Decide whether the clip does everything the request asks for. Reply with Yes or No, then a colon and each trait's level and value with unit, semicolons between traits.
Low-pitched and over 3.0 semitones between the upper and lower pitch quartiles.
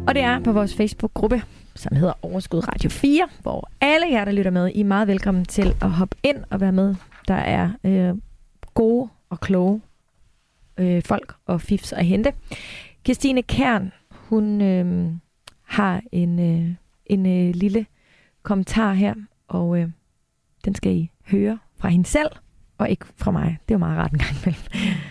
No: high, 195 Hz; average, 3.4 semitones